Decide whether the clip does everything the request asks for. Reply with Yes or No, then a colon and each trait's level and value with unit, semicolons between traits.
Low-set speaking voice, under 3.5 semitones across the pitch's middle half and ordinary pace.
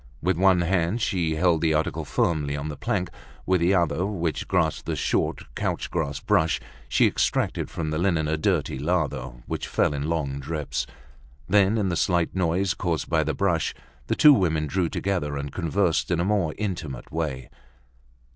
Yes: very low, 85 Hz; average, 3.1 semitones; average, 180 wpm